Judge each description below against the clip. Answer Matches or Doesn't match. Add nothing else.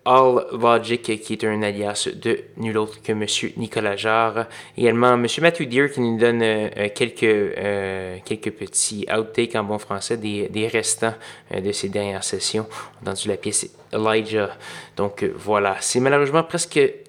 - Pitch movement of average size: Doesn't match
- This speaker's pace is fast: Doesn't match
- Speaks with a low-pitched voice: Matches